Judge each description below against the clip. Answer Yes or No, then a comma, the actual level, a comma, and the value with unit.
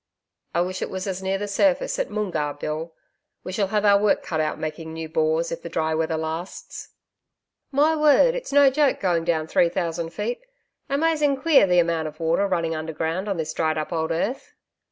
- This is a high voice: No, medium, 175 Hz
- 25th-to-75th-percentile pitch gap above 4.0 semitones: Yes, average, 4.8 semitones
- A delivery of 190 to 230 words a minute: Yes, average, 200 wpm